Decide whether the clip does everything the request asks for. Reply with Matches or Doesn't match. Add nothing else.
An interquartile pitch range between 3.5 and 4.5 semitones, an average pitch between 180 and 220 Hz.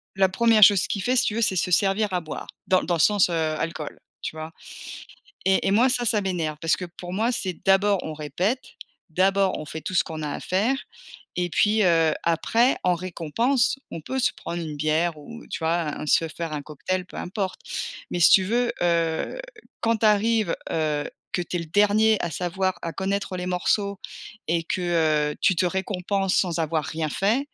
Matches